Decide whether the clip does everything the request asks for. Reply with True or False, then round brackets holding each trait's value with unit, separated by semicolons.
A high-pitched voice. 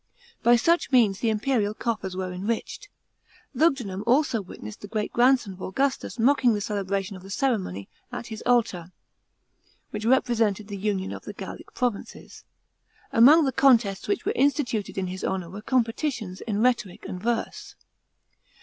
True (220 Hz)